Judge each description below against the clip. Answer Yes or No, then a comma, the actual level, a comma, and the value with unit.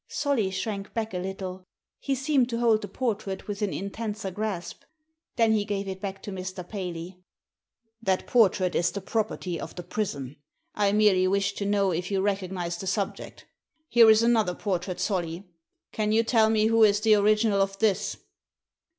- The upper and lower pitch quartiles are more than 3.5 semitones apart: No, average, 2.7 semitones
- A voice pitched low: No, high, 200 Hz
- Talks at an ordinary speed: Yes, average, 180 wpm